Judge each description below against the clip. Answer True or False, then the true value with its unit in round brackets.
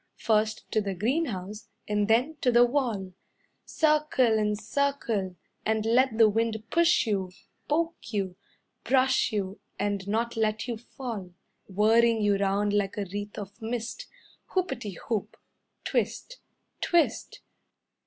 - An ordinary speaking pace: False (130 wpm)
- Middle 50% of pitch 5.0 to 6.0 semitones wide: False (3.4 semitones)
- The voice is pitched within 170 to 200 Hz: False (220 Hz)